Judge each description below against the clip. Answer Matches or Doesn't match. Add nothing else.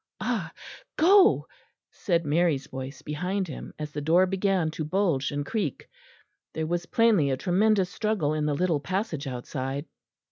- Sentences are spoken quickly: Doesn't match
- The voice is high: Doesn't match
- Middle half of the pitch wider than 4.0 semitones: Matches